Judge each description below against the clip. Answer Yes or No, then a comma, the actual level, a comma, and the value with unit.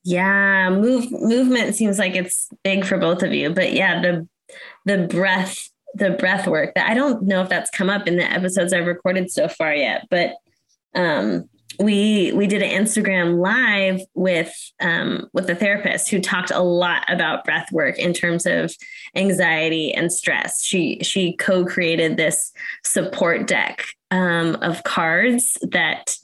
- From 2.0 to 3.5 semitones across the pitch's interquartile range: Yes, narrow, 2.5 semitones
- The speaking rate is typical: Yes, average, 160 wpm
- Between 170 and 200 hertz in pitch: Yes, high, 190 Hz